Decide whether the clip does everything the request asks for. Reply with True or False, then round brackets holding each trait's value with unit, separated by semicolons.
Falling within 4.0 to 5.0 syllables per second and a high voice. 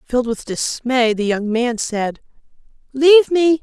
True (4.4 syllables/s; 255 Hz)